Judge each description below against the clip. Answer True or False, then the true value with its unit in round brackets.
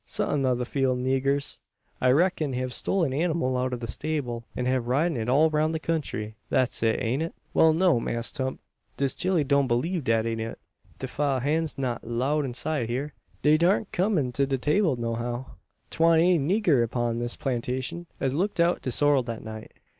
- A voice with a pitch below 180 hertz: True (135 Hz)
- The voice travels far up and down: False (4.4 semitones)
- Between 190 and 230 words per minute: True (205 wpm)